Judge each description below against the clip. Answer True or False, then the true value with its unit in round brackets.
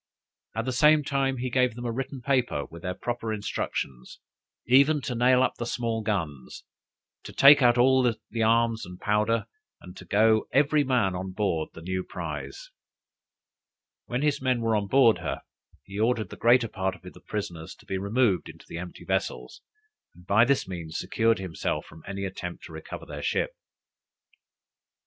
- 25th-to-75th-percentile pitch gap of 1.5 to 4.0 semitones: False (5.3 semitones)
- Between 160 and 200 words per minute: True (175 wpm)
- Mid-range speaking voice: False (115 Hz)